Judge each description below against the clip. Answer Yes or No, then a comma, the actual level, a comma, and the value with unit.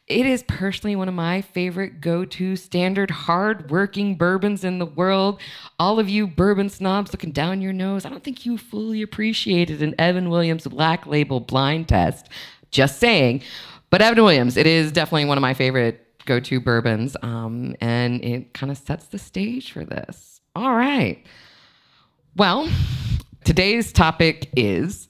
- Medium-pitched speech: Yes, medium, 175 Hz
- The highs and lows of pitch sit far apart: Yes, wide, 6.2 semitones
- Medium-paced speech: Yes, average, 165 wpm